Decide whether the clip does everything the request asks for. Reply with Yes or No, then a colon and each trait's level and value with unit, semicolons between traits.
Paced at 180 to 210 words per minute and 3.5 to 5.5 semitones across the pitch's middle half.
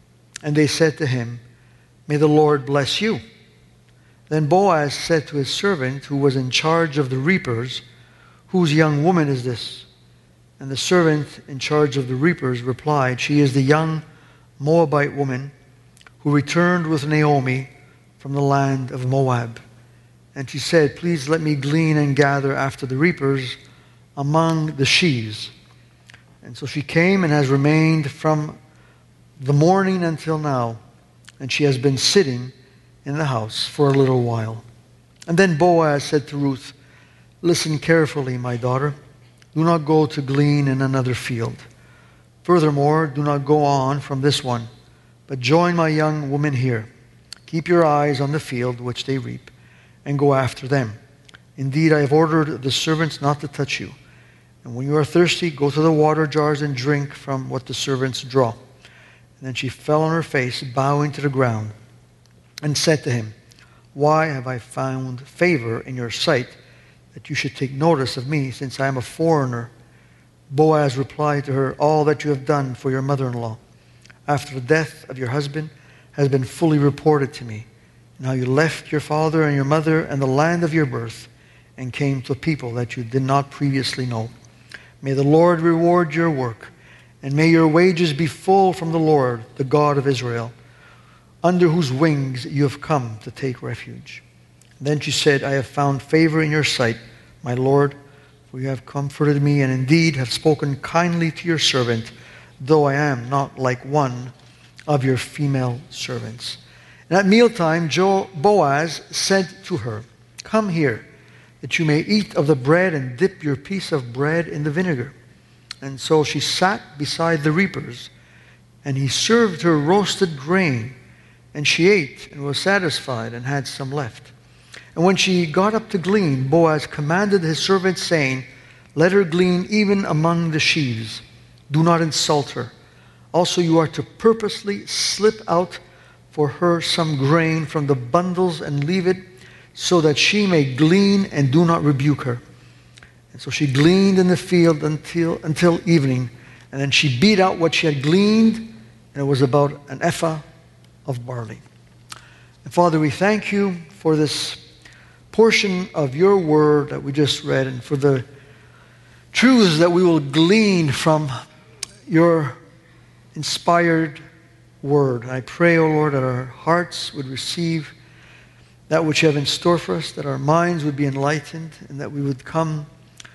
No: average, 170 wpm; average, 3.9 semitones